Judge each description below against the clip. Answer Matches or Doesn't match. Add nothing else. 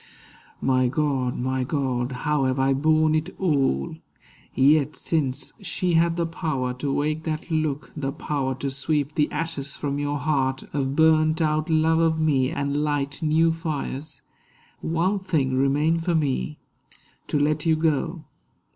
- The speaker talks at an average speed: Matches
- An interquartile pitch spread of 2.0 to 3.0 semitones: Matches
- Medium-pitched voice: Matches